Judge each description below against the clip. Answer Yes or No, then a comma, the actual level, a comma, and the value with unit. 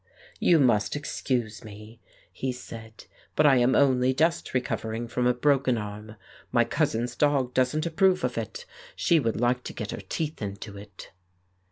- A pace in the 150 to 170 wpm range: Yes, average, 165 wpm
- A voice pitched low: Yes, low, 125 Hz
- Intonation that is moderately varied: Yes, average, 4.4 semitones